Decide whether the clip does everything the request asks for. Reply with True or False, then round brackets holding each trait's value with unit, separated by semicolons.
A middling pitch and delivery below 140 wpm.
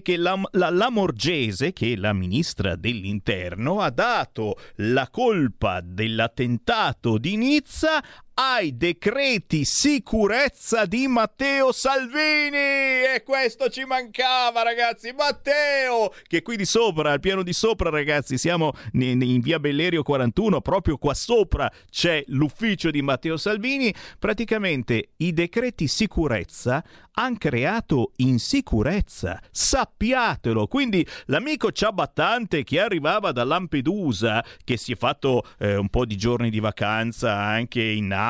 True (170 Hz; 125 wpm)